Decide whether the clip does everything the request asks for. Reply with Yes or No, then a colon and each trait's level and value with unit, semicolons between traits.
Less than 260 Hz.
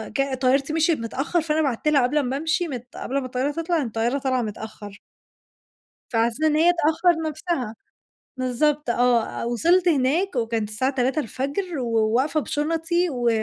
No: very high, 275 Hz